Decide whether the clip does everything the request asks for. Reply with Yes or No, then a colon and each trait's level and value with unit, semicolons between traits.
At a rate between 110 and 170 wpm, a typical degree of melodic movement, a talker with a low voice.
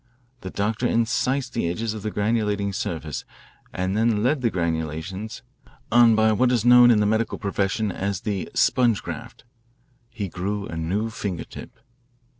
Yes: average, 160 wpm; average, 3.2 semitones; low, 105 Hz